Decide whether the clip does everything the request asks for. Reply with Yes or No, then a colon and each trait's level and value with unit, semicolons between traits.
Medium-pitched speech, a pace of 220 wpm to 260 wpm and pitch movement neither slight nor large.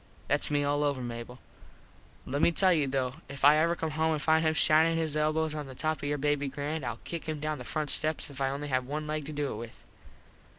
No: medium, 150 Hz; fast, 255 wpm; narrow, 2.1 semitones